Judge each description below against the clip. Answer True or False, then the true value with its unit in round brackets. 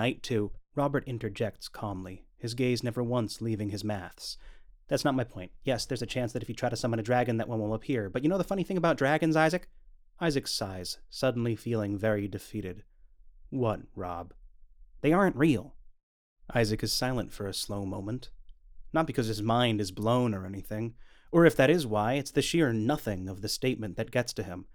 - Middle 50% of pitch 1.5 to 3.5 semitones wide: False (4.2 semitones)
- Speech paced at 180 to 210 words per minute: True (200 wpm)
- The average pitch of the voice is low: True (110 Hz)